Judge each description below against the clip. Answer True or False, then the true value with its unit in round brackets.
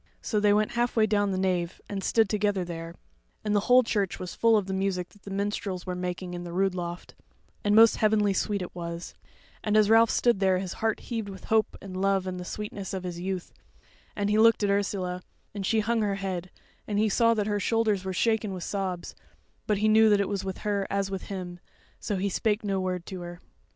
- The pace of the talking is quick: True (230 wpm)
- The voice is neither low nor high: False (200 Hz)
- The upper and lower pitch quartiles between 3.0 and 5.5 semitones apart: False (2.4 semitones)